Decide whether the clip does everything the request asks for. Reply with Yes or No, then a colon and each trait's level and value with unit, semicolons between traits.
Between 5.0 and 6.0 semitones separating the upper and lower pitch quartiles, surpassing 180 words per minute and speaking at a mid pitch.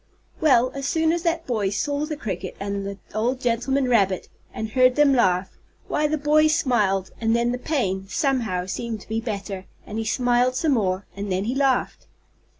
No: wide, 5.6 semitones; average, 190 wpm; high, 240 Hz